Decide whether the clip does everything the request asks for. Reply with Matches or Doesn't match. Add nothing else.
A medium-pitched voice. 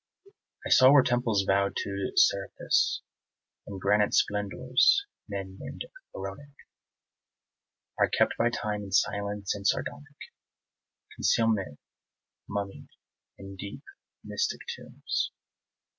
Doesn't match